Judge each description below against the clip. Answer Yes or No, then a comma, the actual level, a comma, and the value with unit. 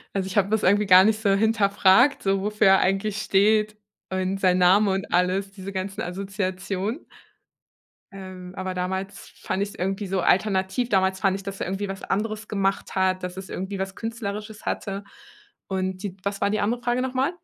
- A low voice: No, high, 195 Hz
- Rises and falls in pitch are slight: Yes, narrow, 1.8 semitones